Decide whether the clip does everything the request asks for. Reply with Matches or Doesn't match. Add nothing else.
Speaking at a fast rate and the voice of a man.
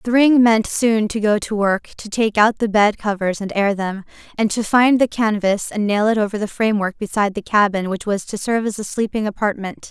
Doesn't match